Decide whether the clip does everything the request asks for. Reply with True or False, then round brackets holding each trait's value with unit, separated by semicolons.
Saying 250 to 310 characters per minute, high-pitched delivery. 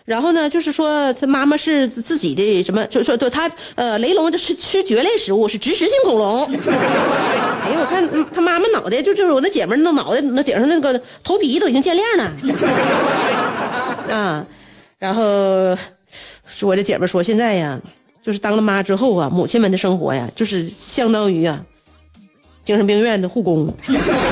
True (265 characters per minute; 250 Hz)